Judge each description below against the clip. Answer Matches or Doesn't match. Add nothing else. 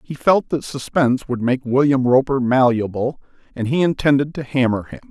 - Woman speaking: Doesn't match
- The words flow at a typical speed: Matches